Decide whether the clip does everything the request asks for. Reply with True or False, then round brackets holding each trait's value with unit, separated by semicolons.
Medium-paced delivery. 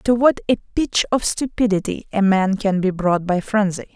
True (195 wpm)